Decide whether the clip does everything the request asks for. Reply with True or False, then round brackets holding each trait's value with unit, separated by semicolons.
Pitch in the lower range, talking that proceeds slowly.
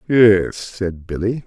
True (105 Hz; 125 wpm)